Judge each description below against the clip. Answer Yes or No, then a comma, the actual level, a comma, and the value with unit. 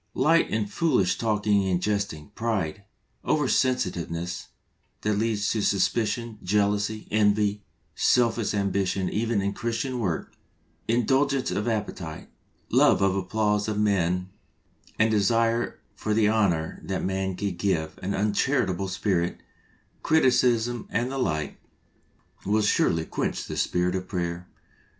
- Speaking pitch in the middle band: No, low, 105 Hz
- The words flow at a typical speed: No, slow, 125 wpm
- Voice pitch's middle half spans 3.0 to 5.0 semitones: Yes, average, 3.3 semitones